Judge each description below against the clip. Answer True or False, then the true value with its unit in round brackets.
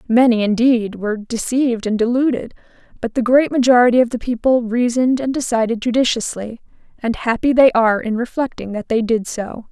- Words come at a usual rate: True (165 wpm)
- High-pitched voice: True (235 Hz)